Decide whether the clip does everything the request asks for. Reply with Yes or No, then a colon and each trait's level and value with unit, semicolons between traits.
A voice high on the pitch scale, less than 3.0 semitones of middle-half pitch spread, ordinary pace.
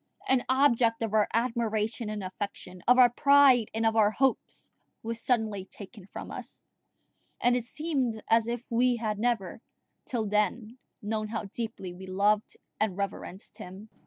Yes: high, 225 Hz; narrow, 2.6 semitones; average, 160 wpm